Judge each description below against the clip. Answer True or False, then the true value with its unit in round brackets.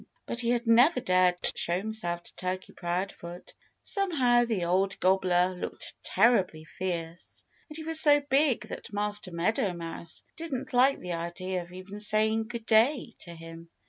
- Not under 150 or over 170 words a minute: True (160 wpm)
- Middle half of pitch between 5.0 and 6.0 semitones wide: True (5.4 semitones)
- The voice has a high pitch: True (195 Hz)